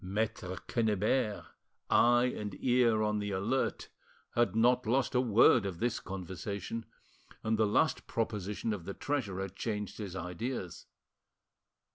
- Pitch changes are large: No, average, 3.3 semitones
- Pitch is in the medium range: No, low, 105 Hz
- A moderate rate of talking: No, slow, 130 wpm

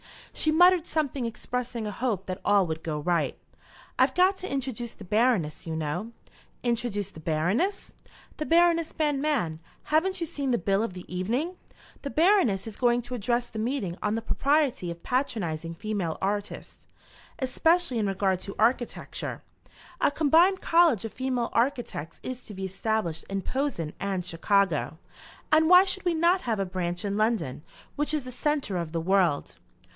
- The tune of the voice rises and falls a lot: Yes, wide, 7.5 semitones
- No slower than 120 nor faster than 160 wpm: No, average, 170 wpm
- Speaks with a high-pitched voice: Yes, high, 230 Hz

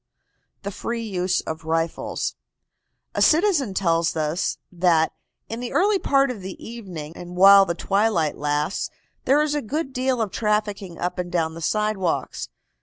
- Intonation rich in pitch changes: Yes, wide, 5.7 semitones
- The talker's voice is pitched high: Yes, high, 195 Hz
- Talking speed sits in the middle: Yes, average, 160 wpm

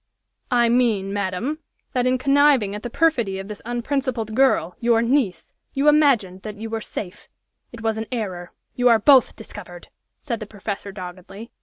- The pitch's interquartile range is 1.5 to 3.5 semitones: No, average, 4.1 semitones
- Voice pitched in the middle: No, high, 225 Hz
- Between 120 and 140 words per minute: No, average, 170 wpm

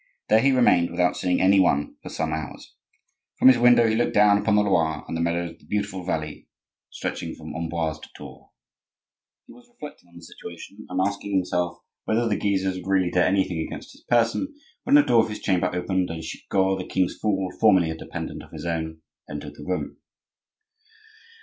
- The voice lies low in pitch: Yes, very low, 95 Hz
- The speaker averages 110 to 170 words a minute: No, average, 200 wpm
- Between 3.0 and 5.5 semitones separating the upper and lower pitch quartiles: Yes, average, 3.7 semitones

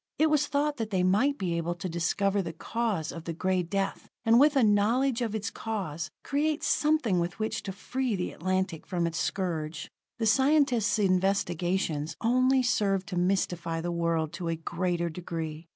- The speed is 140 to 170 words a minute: No, average, 180 wpm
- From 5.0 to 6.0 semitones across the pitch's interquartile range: Yes, wide, 5.4 semitones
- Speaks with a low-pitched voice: No, high, 190 Hz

